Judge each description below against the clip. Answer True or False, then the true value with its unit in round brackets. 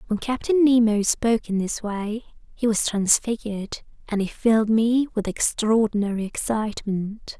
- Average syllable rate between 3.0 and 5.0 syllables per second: True (4.8 syllables/s)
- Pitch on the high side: True (220 Hz)